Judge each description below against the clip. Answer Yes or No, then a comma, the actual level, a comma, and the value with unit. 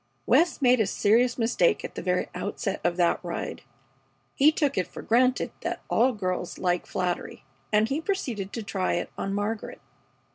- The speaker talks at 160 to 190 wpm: Yes, average, 175 wpm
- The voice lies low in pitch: No, high, 220 Hz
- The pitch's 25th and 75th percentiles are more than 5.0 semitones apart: Yes, wide, 5.4 semitones